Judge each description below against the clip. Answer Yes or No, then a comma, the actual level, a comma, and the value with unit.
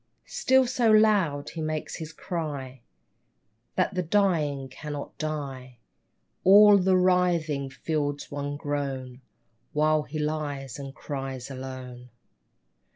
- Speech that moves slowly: Yes, slow, 110 wpm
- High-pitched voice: No, medium, 150 Hz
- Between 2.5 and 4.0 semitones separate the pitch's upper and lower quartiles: No, average, 4.4 semitones